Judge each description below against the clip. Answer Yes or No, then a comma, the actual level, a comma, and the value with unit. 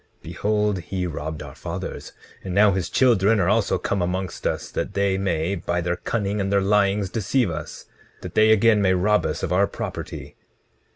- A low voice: Yes, low, 100 Hz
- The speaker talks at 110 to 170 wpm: No, average, 185 wpm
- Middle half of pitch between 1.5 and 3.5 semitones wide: Yes, narrow, 2.6 semitones